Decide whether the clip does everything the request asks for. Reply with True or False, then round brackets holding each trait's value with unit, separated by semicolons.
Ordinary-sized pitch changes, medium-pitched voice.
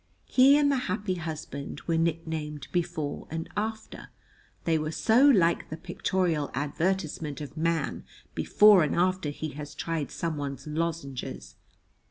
True (3.5 semitones; 165 Hz)